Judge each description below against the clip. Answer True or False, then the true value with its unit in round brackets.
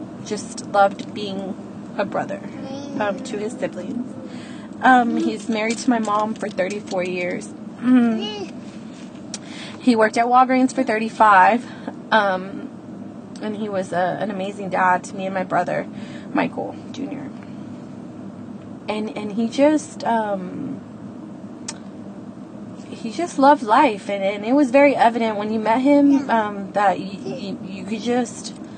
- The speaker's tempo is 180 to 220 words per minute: False (140 wpm)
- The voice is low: False (225 Hz)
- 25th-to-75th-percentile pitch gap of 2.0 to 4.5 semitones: True (3.8 semitones)